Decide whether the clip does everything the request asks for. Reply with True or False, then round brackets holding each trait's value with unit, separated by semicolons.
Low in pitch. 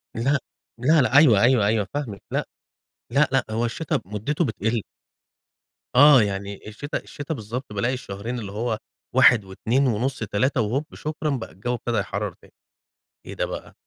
True (120 Hz)